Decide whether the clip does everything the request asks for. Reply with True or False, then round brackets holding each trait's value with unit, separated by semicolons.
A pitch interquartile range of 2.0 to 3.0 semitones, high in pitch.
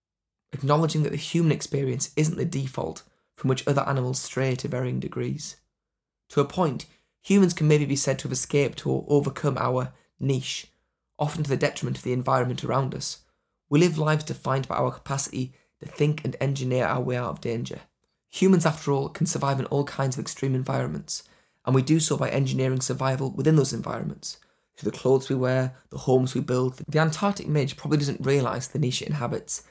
False (2.7 semitones; 135 Hz)